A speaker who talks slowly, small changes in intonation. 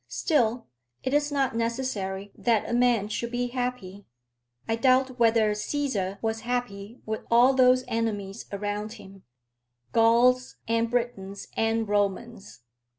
No: slow, 130 wpm; average, 3.2 semitones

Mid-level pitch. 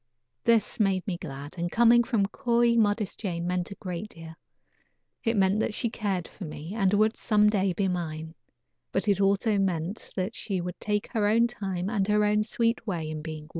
No: high, 195 Hz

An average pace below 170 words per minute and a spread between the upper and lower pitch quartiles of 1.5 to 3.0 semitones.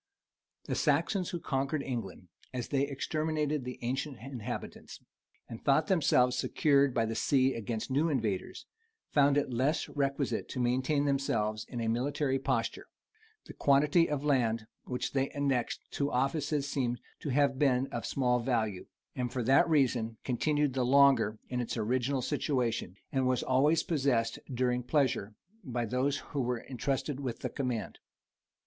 Yes: average, 155 wpm; average, 2.7 semitones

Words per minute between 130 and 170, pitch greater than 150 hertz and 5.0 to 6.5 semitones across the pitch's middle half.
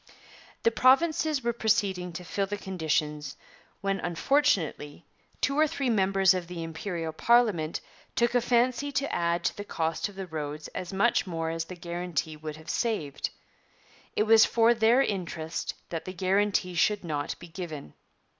Yes: average, 165 wpm; medium, 185 Hz; wide, 5.5 semitones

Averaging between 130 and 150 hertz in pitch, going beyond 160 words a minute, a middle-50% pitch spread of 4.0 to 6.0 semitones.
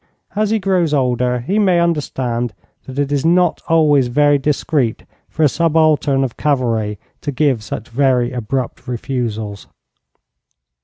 No: low, 135 Hz; average, 140 wpm; average, 4.3 semitones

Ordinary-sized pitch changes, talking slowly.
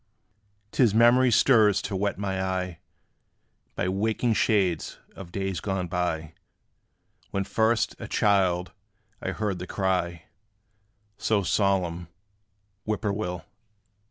Yes: average, 3.0 semitones; slow, 120 wpm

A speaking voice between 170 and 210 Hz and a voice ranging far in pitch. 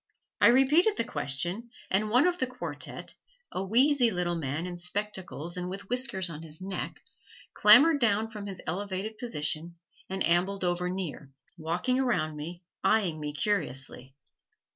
No: high, 190 Hz; average, 5.0 semitones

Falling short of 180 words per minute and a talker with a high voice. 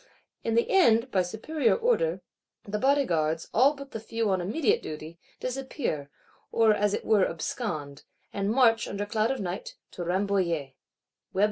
Yes: average, 150 wpm; high, 215 Hz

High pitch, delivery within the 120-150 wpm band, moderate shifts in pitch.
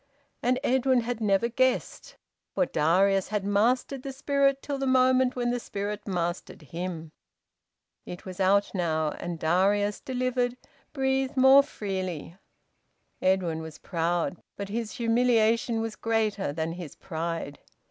No: high, 210 Hz; slow, 135 wpm; wide, 6.1 semitones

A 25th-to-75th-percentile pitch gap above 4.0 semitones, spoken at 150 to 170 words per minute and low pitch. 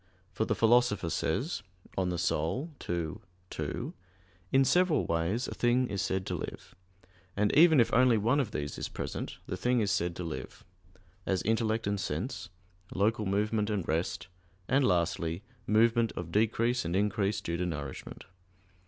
Yes: average, 5.1 semitones; average, 160 wpm; low, 105 Hz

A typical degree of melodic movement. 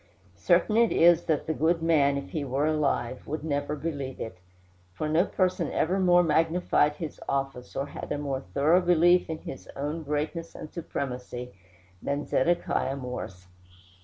Yes: average, 3.3 semitones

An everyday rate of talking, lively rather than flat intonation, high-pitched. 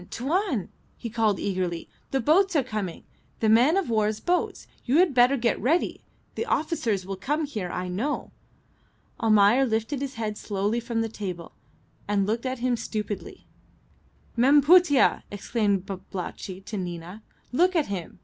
Yes: average, 155 wpm; wide, 5.7 semitones; high, 225 Hz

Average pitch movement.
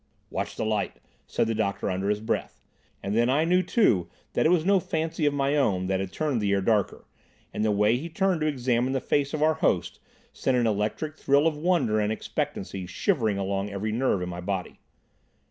No: wide, 7.3 semitones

